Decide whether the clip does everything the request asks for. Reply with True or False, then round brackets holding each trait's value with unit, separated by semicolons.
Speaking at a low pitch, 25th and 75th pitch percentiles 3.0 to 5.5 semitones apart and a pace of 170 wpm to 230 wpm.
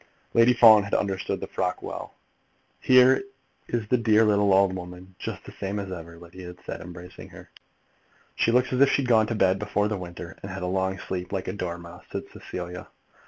True (95 Hz; 3.4 semitones; 205 wpm)